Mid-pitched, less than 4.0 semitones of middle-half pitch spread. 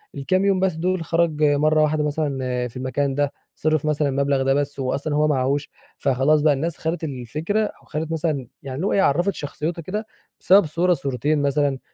Yes: medium, 150 Hz; average, 2.8 semitones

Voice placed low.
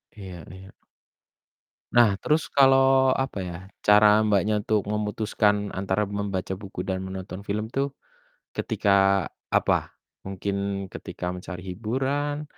Yes: low, 100 Hz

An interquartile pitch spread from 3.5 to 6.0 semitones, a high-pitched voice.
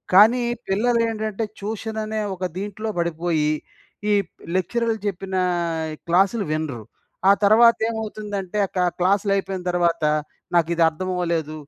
Yes: average, 3.9 semitones; high, 195 Hz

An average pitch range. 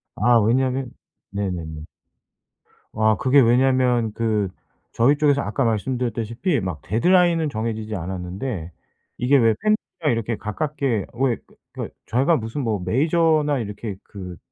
Yes: average, 4.5 semitones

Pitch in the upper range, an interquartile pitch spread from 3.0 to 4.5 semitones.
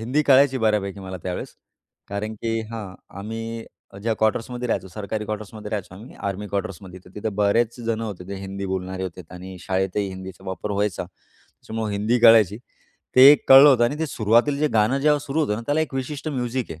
No: low, 110 Hz; average, 3.7 semitones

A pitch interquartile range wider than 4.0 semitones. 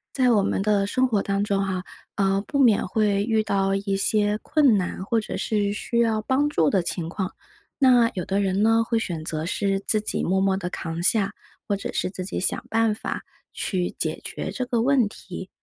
No: average, 2.8 semitones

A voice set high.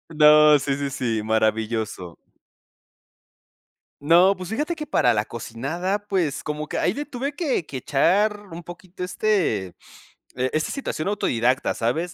No: medium, 150 Hz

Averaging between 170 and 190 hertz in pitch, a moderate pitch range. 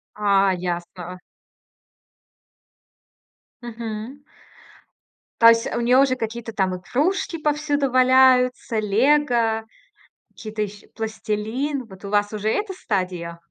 No: high, 225 Hz; average, 4.0 semitones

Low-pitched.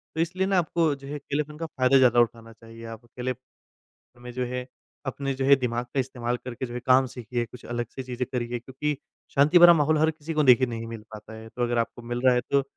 Yes: low, 125 Hz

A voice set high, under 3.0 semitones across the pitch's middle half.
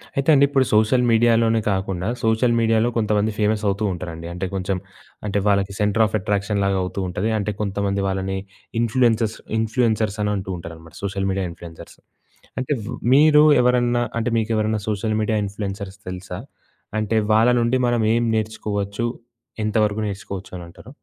No: low, 105 Hz; narrow, 2.6 semitones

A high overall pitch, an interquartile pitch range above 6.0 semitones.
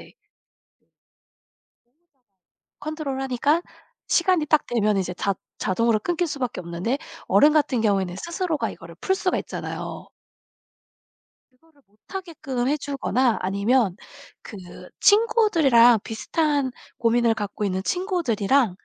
Yes: very high, 260 Hz; wide, 6.7 semitones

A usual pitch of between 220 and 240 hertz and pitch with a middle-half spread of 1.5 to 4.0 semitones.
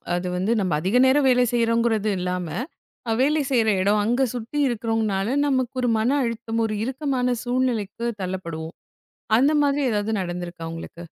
No: high, 225 Hz; average, 4.8 semitones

